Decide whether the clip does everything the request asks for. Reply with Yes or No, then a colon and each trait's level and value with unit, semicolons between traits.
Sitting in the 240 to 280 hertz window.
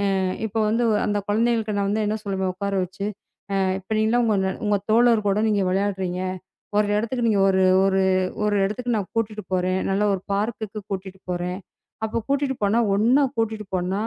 No: high, 205 Hz